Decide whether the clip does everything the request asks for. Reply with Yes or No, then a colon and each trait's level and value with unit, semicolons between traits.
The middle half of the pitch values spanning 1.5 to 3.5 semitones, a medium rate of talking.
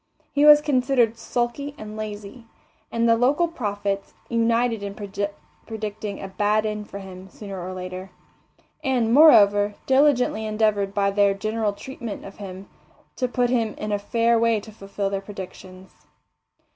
Yes: average, 2.9 semitones; average, 150 wpm